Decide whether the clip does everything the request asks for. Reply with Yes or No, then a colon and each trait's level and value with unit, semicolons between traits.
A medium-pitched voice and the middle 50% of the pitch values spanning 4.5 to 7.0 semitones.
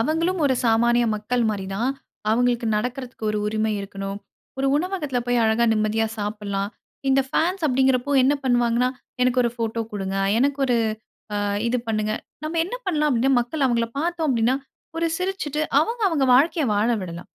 No: high, 245 Hz; average, 4.8 semitones